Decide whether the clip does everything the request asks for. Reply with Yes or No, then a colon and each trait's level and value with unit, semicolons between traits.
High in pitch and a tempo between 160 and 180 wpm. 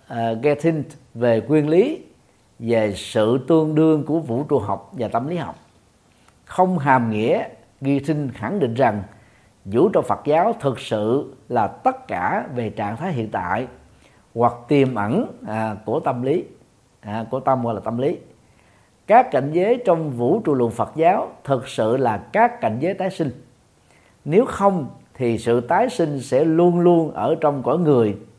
No: low, 135 Hz; average, 170 wpm